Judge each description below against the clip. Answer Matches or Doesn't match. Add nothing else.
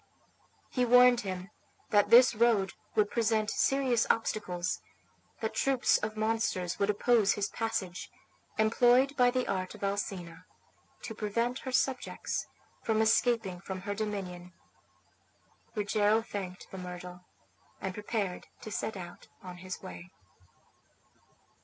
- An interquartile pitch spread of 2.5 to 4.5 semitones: Matches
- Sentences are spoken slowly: Matches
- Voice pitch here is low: Doesn't match